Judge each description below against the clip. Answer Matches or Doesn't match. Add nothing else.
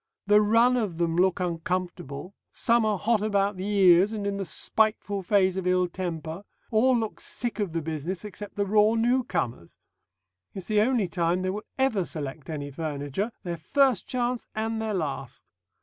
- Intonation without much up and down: Doesn't match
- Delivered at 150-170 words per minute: Doesn't match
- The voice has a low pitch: Doesn't match